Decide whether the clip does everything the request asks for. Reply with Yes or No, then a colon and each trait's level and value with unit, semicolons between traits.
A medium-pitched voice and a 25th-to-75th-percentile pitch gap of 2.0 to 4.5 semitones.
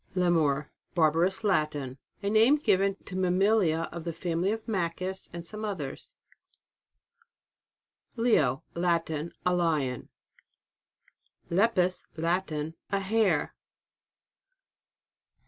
Yes: medium, 175 Hz; average, 3.6 semitones